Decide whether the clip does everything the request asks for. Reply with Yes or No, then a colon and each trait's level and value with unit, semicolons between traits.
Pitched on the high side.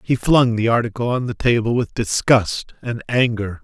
No: low, 115 Hz